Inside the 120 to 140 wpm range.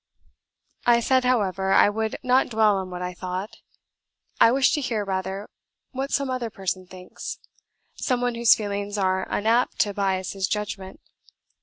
No: average, 160 wpm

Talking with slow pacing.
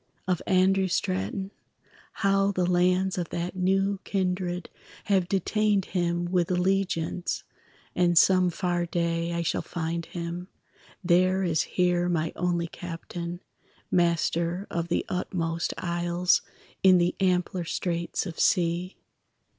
Yes: slow, 125 wpm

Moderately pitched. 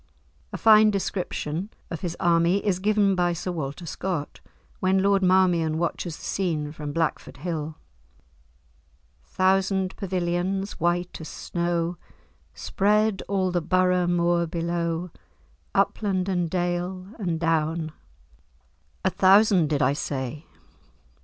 Yes: medium, 175 Hz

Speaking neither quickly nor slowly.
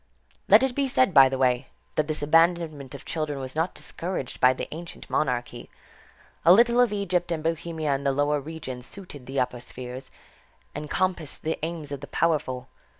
Yes: average, 185 wpm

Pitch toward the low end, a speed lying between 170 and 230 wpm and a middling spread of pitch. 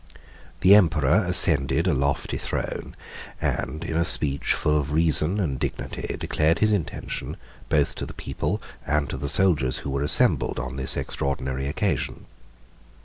No: very low, 75 Hz; average, 150 wpm; average, 3.5 semitones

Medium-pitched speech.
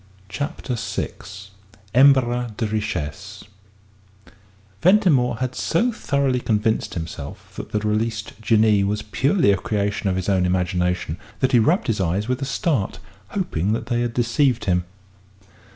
No: low, 110 Hz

